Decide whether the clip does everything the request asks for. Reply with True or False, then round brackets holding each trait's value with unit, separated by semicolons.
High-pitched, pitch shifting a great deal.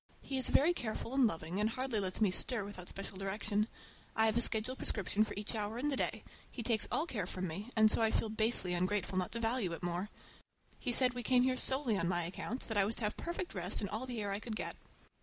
False (215 Hz; 3.9 semitones)